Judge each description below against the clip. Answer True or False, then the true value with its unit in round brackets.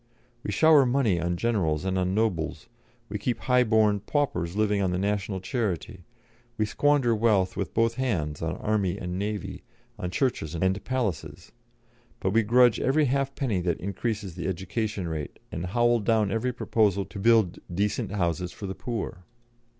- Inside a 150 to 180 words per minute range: True (165 wpm)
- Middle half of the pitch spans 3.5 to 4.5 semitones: True (4.2 semitones)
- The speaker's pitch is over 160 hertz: False (105 Hz)